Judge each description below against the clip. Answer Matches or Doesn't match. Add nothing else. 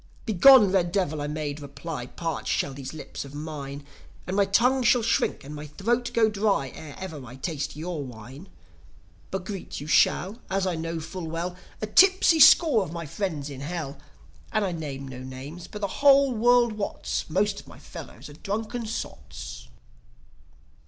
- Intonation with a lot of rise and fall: Matches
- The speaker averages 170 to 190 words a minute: Matches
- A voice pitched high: Doesn't match